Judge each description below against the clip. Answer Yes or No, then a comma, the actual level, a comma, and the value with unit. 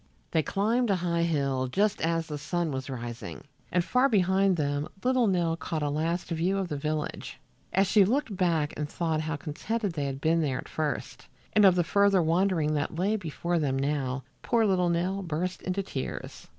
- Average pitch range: Yes, average, 4.4 semitones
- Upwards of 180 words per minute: Yes, average, 195 wpm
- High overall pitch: No, medium, 170 Hz